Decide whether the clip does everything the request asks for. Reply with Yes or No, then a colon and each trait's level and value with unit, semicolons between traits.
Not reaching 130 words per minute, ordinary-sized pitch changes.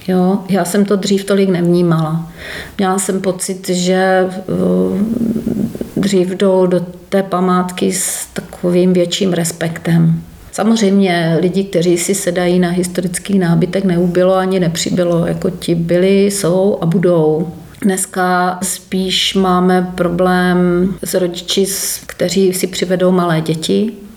No: average, 120 wpm; narrow, 1.5 semitones